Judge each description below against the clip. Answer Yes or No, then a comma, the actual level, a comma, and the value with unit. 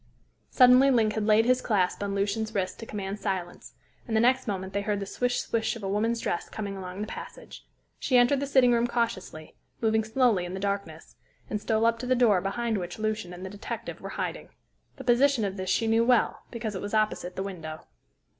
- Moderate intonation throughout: Yes, average, 3.4 semitones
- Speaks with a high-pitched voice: Yes, high, 215 Hz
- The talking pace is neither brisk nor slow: No, fast, 220 wpm